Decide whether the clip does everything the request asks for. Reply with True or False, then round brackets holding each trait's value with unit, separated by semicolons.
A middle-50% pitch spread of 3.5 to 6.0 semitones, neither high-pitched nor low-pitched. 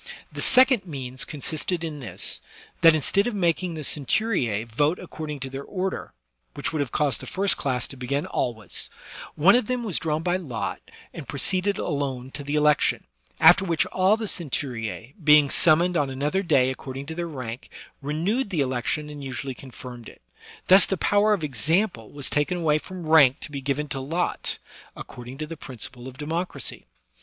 True (4.9 semitones; 150 Hz)